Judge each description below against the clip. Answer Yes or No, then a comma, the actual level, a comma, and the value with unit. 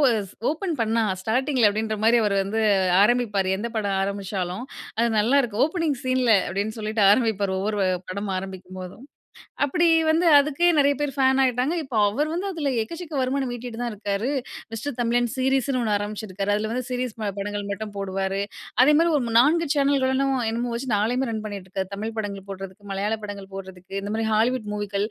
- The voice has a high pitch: Yes, high, 225 Hz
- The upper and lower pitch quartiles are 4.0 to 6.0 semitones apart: Yes, average, 4.5 semitones